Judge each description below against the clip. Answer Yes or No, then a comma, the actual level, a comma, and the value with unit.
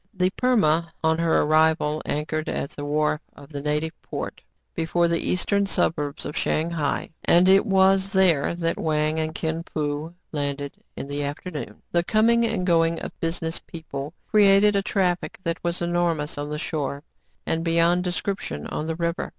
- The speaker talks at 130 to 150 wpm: No, average, 175 wpm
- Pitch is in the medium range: Yes, medium, 165 Hz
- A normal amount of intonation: Yes, average, 3.0 semitones